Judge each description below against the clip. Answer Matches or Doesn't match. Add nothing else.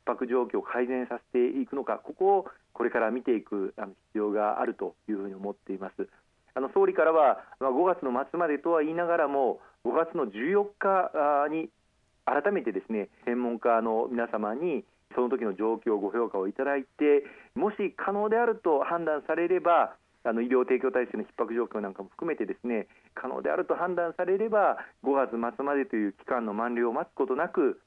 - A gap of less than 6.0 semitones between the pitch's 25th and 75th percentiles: Doesn't match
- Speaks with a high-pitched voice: Doesn't match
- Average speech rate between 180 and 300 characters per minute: Doesn't match